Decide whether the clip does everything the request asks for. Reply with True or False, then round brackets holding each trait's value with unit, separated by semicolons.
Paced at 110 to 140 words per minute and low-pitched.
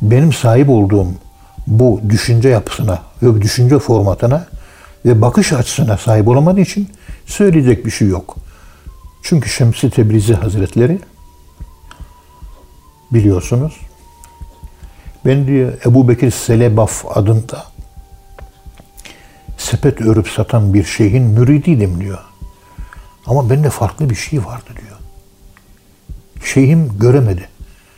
False (100 wpm; 110 Hz)